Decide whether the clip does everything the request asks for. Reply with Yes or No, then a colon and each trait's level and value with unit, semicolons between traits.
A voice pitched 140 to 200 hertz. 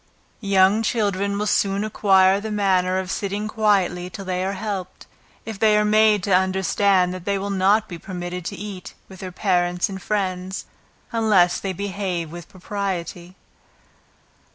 Yes: high, 190 Hz